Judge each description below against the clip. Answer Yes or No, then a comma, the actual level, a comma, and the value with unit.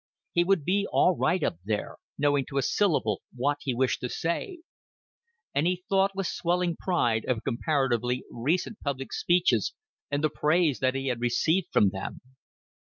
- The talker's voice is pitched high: No, medium, 145 Hz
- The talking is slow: No, average, 165 wpm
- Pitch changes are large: Yes, wide, 6.1 semitones